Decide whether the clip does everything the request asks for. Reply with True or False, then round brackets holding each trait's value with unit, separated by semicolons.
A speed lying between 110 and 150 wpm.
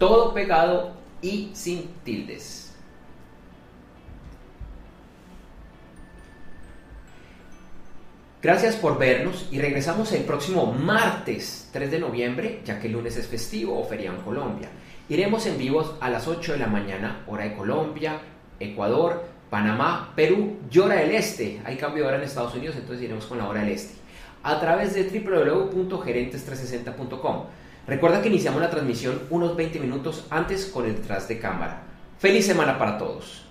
True (145 wpm)